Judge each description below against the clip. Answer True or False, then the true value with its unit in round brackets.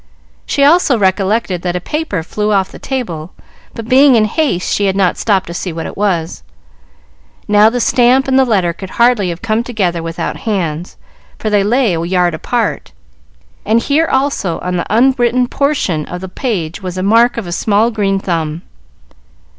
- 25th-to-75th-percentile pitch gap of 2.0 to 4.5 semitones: False (5.2 semitones)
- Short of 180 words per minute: False (185 wpm)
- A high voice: True (205 Hz)